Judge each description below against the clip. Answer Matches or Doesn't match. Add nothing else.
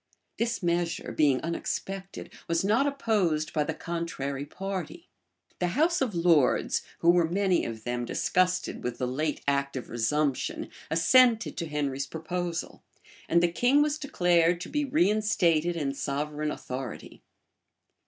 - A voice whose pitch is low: Doesn't match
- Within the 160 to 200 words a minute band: Doesn't match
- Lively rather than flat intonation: Doesn't match